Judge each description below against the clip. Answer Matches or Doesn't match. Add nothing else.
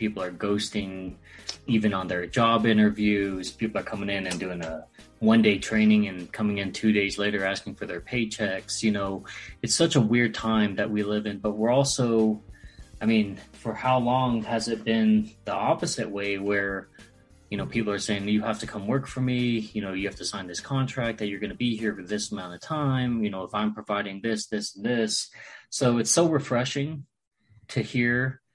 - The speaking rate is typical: Doesn't match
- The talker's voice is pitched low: Matches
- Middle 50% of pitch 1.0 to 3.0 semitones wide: Matches